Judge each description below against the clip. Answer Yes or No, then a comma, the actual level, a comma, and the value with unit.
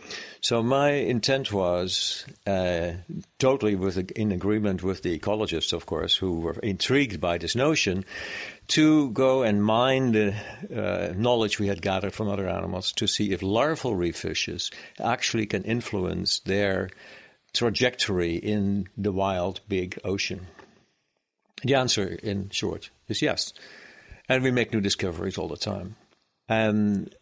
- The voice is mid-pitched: No, low, 100 Hz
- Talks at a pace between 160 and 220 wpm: No, average, 145 wpm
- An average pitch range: Yes, average, 3.7 semitones